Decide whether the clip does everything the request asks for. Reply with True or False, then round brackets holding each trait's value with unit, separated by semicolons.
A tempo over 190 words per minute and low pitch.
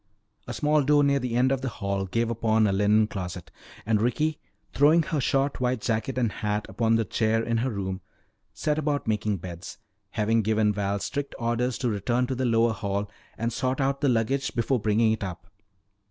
True (200 wpm; 115 Hz)